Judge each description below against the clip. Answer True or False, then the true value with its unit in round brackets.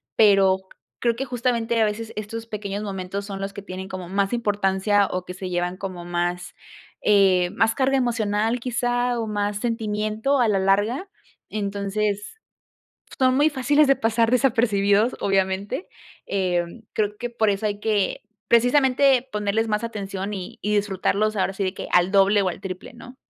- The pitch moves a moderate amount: True (3.1 semitones)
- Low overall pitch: False (210 Hz)